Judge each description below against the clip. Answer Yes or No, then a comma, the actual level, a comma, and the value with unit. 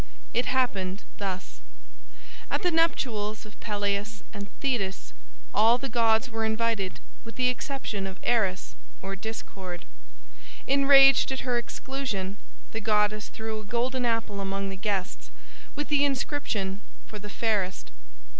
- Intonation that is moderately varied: Yes, average, 4.2 semitones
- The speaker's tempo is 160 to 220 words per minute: No, slow, 135 wpm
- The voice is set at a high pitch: Yes, high, 220 Hz